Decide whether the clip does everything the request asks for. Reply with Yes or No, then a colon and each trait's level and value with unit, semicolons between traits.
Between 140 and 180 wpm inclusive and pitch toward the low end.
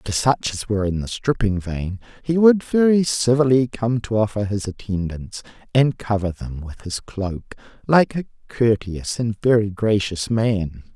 Yes: average, 165 wpm; low, 110 Hz